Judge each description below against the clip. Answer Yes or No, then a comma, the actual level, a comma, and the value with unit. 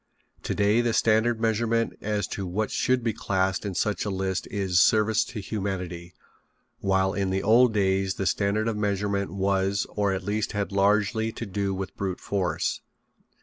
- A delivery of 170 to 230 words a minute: Yes, average, 175 wpm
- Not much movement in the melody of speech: Yes, narrow, 2.1 semitones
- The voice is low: Yes, low, 100 Hz